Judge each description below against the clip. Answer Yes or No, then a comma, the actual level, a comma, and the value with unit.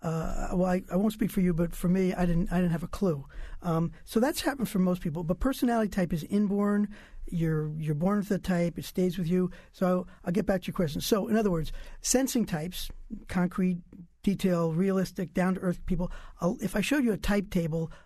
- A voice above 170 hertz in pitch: Yes, medium, 185 Hz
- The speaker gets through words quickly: Yes, fast, 225 wpm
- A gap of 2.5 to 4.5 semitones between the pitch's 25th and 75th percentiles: Yes, average, 2.8 semitones